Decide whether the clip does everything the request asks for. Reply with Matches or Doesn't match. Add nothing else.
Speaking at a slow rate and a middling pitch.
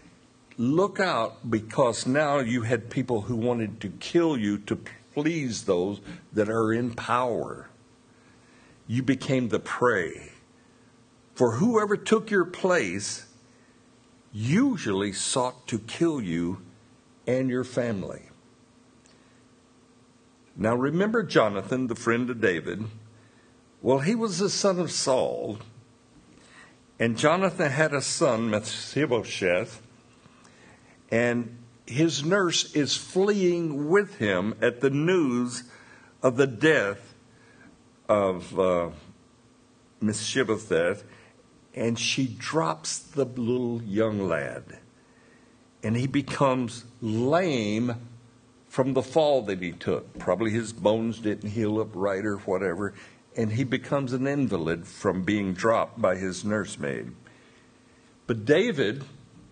Doesn't match